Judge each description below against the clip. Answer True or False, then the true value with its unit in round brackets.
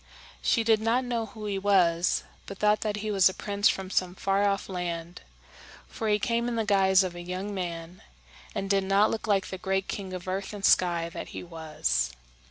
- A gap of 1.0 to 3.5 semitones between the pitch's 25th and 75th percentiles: True (2.7 semitones)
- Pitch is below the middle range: False (195 Hz)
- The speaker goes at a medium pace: False (210 wpm)